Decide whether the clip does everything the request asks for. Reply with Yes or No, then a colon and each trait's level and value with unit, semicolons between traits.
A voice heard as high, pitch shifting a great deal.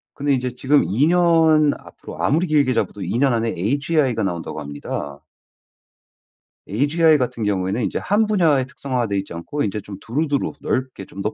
No: low, 130 Hz; wide, 6.5 semitones